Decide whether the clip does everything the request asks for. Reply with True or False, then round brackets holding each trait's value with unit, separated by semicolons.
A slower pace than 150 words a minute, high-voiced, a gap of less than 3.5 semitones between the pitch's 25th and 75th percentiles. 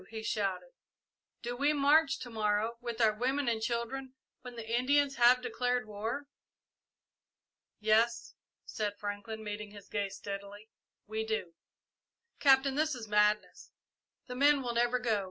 True (140 wpm; 230 Hz; 3.1 semitones)